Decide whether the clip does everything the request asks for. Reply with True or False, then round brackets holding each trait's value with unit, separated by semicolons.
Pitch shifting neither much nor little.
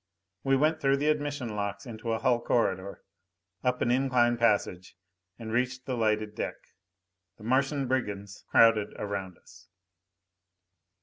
True (3.9 semitones)